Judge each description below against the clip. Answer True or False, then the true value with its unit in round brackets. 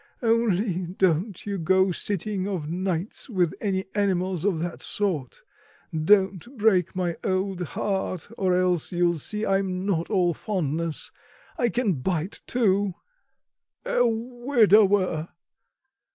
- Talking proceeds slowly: True (120 wpm)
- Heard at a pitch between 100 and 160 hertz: False (190 Hz)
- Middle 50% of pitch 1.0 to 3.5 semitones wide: True (2.8 semitones)